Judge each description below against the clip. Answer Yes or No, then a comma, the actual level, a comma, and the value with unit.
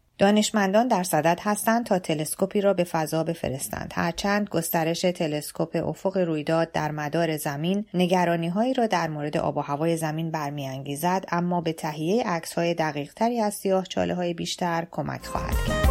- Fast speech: Yes, fast, 160 wpm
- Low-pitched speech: No, medium, 170 Hz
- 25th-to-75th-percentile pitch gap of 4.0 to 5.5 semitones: No, average, 3.6 semitones